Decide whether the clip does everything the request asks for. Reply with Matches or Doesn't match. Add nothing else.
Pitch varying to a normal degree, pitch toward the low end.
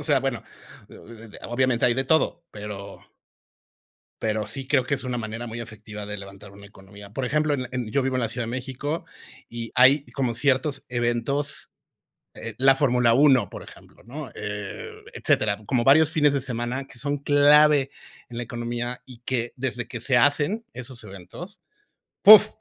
Matches